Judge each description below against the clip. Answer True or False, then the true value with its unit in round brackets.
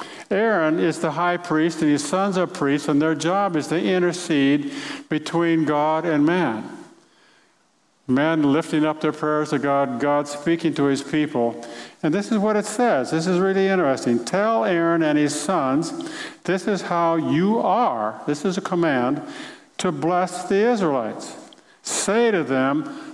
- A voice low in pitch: False (165 Hz)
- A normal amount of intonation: True (4.5 semitones)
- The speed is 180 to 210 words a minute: False (165 wpm)